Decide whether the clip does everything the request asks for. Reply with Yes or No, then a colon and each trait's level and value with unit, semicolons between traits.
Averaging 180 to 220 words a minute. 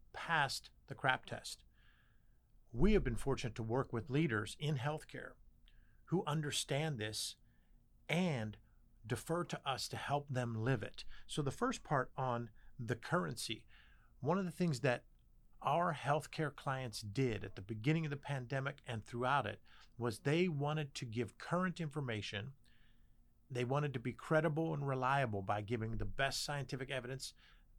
No: average, 155 wpm